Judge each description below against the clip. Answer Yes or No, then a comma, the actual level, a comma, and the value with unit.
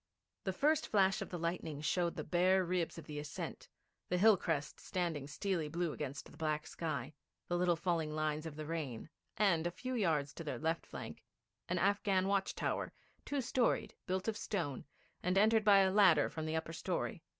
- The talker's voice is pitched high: No, medium, 175 Hz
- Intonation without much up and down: No, average, 3.8 semitones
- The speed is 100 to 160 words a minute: No, average, 195 wpm